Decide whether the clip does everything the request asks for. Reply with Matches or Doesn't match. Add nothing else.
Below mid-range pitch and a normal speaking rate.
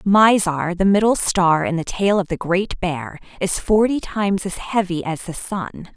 Doesn't match